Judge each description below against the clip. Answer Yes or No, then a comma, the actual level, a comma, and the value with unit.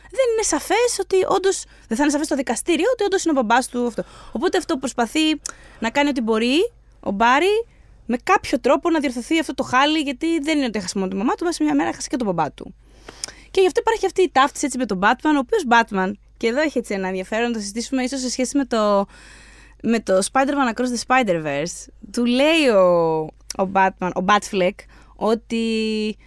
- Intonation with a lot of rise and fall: Yes, wide, 6.1 semitones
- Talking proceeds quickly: Yes, fast, 210 wpm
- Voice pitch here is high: Yes, very high, 255 Hz